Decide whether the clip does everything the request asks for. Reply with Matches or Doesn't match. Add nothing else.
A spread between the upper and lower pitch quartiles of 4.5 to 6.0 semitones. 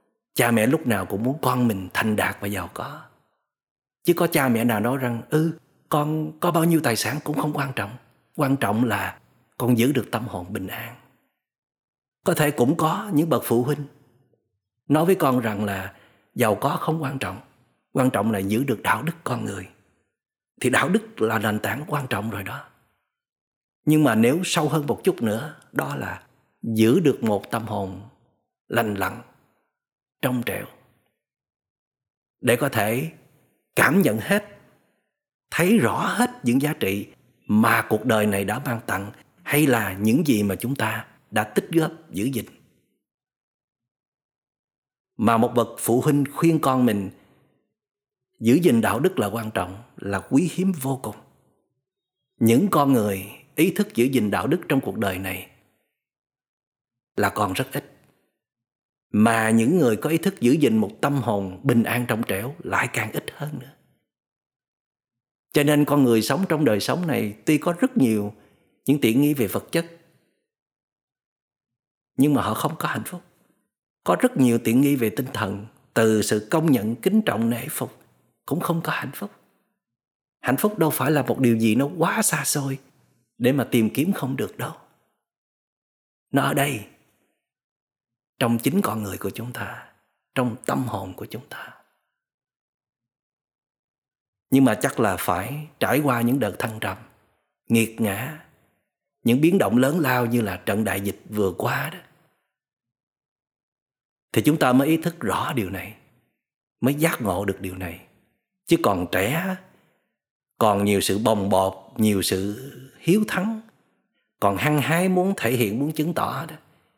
Matches